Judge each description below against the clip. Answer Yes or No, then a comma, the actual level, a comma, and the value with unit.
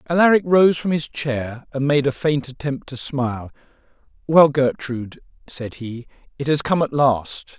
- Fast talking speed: No, average, 165 wpm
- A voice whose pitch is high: No, medium, 140 Hz